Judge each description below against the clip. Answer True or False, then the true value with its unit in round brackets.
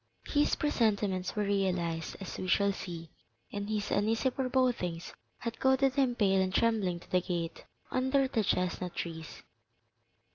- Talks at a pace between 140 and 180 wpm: True (145 wpm)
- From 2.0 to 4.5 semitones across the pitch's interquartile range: False (5.2 semitones)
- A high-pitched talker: True (200 Hz)